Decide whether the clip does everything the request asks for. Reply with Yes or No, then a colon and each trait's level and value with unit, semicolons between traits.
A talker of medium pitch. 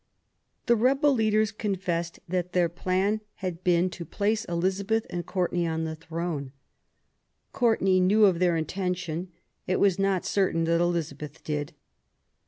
Yes: medium, 180 Hz